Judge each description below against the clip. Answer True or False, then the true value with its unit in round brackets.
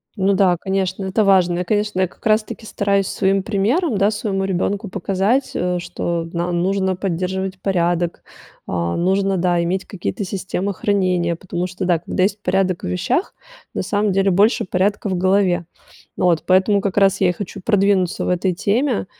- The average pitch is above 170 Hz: True (190 Hz)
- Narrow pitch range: True (1.9 semitones)